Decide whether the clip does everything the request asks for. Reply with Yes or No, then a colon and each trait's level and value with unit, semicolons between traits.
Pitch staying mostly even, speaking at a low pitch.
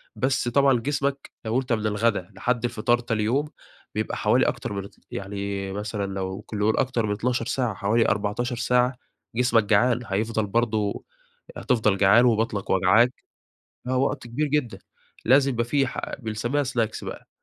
No: average, 3.3 semitones; low, 115 Hz